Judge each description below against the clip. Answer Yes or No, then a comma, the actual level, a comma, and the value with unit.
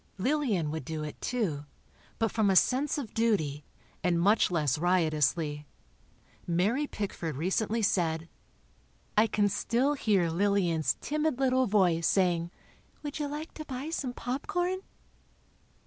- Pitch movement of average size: No, wide, 7.5 semitones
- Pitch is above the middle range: Yes, high, 200 Hz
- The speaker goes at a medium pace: No, slow, 130 wpm